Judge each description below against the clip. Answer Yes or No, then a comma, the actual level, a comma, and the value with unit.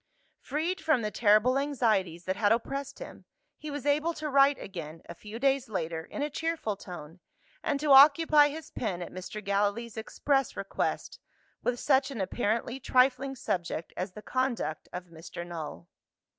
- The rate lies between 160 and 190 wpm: Yes, average, 165 wpm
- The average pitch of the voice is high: Yes, high, 240 Hz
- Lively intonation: Yes, wide, 7.0 semitones